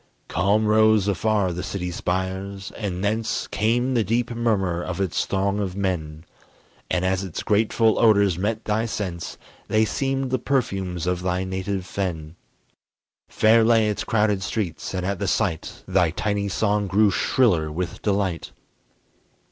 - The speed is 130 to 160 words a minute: Yes, average, 150 wpm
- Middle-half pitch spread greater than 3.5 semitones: No, average, 3.0 semitones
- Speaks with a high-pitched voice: No, low, 100 Hz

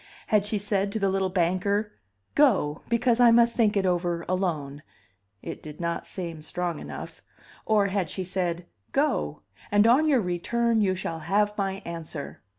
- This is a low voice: No, high, 190 Hz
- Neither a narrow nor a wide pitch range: Yes, average, 3.7 semitones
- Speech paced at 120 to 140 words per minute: No, average, 165 wpm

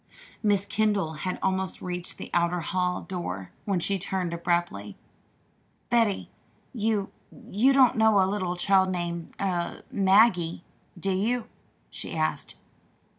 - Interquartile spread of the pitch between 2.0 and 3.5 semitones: Yes, average, 2.9 semitones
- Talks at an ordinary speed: No, slow, 125 wpm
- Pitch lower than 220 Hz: Yes, high, 190 Hz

